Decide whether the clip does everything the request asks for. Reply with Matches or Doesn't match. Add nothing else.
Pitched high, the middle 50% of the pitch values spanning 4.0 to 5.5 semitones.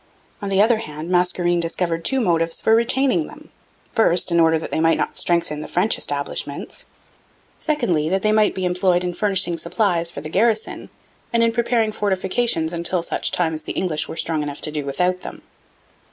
Doesn't match